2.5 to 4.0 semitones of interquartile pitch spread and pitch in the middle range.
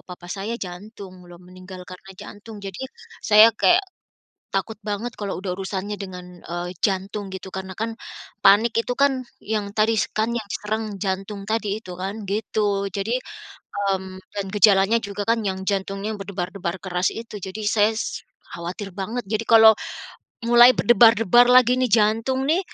No: average, 2.8 semitones; high, 205 Hz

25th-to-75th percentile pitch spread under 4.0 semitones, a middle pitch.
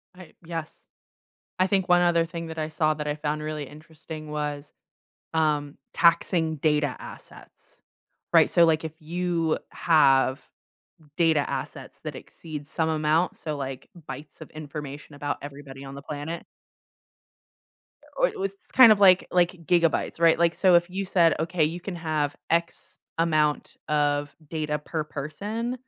Yes: narrow, 2.4 semitones; medium, 155 Hz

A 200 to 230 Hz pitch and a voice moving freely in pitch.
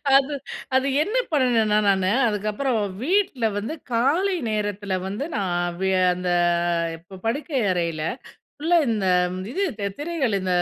Yes: high, 220 Hz; wide, 6.7 semitones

